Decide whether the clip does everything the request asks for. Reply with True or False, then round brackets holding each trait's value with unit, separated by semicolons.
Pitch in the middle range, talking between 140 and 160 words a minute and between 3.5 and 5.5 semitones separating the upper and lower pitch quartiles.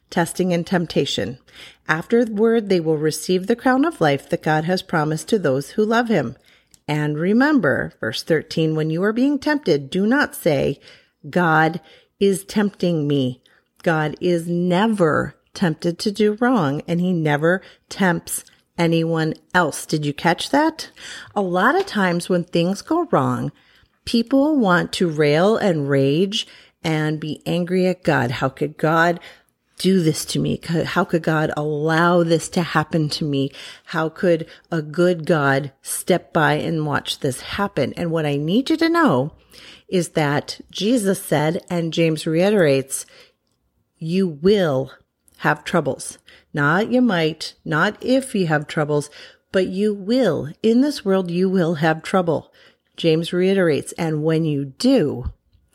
True (175 Hz; 155 wpm; 4.4 semitones)